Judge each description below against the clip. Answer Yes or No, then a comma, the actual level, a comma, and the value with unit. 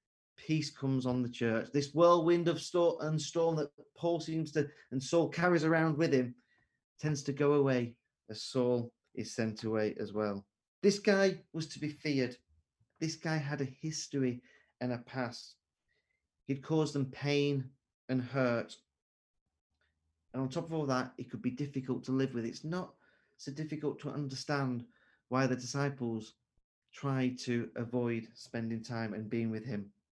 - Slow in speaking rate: No, average, 165 wpm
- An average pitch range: Yes, average, 4.4 semitones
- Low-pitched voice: Yes, low, 130 Hz